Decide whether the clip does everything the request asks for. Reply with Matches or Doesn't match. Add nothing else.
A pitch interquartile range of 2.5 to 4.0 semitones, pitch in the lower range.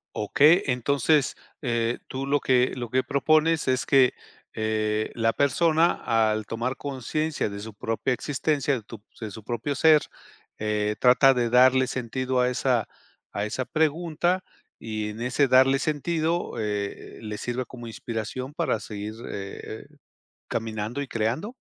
Doesn't match